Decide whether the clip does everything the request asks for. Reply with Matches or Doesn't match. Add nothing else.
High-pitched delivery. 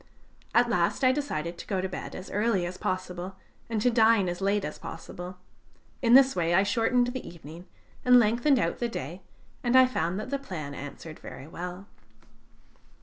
Matches